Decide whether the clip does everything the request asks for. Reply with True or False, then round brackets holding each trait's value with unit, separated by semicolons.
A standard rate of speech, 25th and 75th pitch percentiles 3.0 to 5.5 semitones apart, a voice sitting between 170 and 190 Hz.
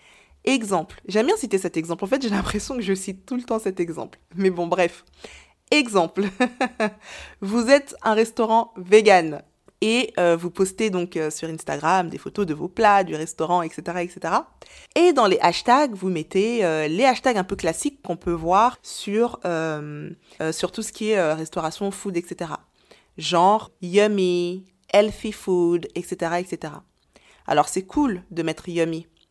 True (170 wpm; 4.1 semitones; 185 Hz)